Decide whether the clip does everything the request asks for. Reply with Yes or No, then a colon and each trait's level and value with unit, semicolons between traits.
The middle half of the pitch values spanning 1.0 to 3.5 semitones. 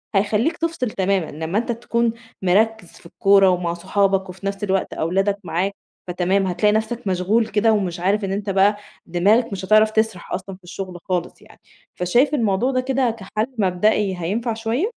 Yes: average, 3.2 semitones